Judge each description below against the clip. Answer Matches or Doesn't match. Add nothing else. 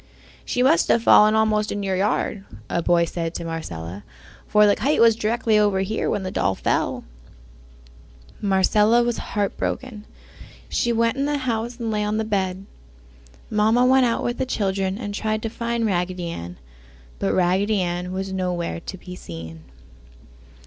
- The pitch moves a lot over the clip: Doesn't match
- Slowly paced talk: Doesn't match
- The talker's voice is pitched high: Matches